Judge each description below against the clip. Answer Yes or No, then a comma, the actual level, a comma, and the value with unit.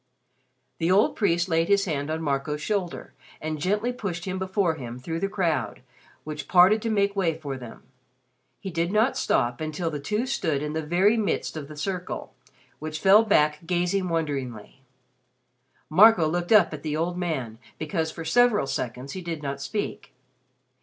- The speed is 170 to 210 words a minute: Yes, average, 175 wpm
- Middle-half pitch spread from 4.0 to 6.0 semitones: Yes, average, 4.5 semitones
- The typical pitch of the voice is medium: Yes, medium, 165 Hz